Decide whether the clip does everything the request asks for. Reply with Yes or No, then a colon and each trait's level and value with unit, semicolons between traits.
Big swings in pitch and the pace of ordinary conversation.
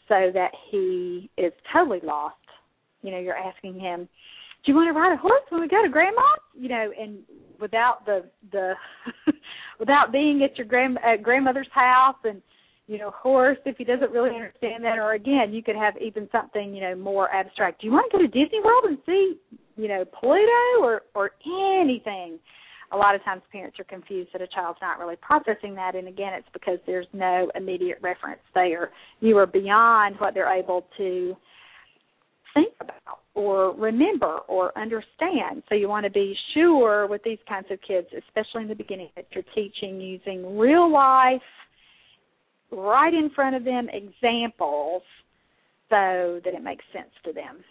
Yes: wide, 6.2 semitones; average, 180 wpm